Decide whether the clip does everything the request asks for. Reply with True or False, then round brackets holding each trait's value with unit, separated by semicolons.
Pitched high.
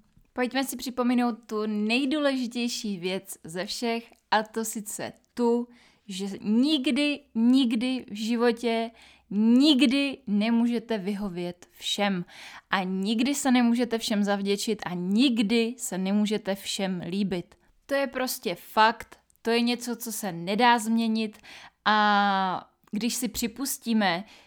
True (225 Hz)